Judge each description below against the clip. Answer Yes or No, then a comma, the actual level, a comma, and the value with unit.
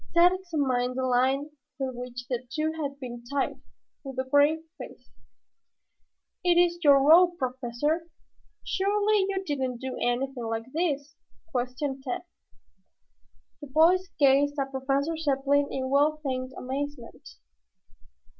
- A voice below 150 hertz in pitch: No, very high, 275 Hz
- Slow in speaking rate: Yes, slow, 125 wpm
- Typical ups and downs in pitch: Yes, average, 3.4 semitones